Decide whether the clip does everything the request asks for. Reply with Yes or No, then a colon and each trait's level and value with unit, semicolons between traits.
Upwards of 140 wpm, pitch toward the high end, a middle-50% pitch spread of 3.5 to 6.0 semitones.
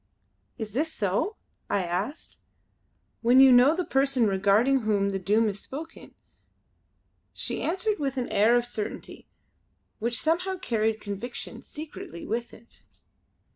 No: slow, 135 wpm; high, 240 Hz; average, 4.9 semitones